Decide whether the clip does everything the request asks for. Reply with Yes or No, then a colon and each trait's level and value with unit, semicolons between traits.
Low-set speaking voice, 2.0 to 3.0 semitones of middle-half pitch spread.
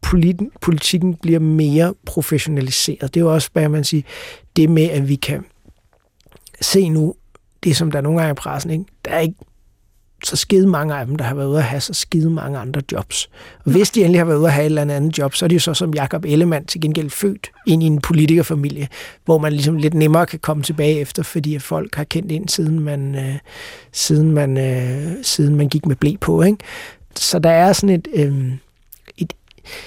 No: medium, 155 Hz; narrow, 2.6 semitones